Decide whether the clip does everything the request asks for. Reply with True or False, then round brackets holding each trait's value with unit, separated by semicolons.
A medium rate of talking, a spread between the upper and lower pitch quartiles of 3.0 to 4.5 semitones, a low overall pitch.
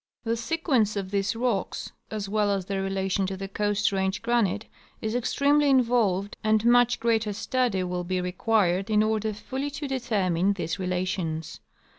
False (160 wpm; 3.5 semitones; 205 Hz)